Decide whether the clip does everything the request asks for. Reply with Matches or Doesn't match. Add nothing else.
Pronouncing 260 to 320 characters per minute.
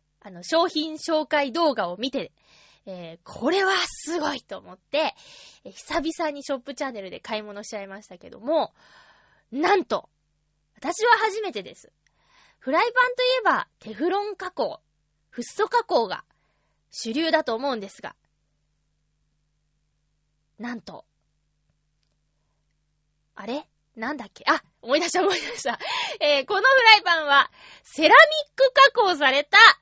Matches